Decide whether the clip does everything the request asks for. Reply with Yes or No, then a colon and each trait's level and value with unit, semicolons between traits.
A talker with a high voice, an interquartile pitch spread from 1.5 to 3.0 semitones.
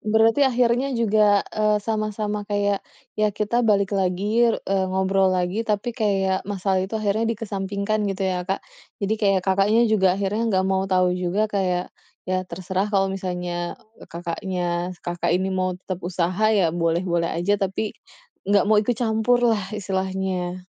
Yes: high, 195 Hz; narrow, 2.4 semitones